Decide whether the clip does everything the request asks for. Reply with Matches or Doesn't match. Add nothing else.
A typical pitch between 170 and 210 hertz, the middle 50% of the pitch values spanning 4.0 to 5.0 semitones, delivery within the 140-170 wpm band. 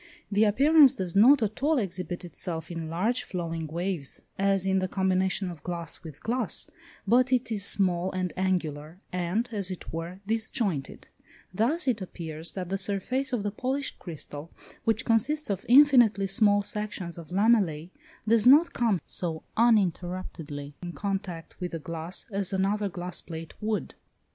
Matches